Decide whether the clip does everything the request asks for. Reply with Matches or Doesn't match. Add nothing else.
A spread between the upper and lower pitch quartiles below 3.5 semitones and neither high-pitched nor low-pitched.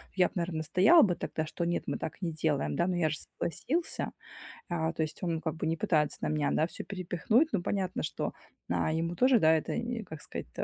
Matches